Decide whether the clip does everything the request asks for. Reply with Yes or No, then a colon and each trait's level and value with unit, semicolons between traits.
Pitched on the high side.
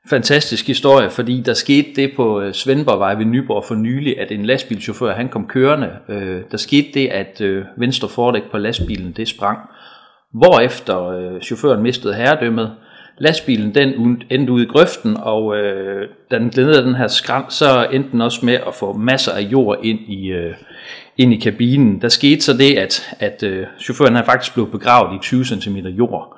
No: low, 120 Hz